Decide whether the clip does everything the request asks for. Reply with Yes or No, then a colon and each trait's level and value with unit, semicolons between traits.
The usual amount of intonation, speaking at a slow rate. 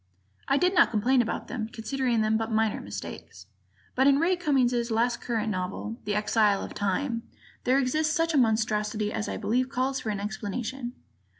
No: average, 3.7 semitones; average, 180 wpm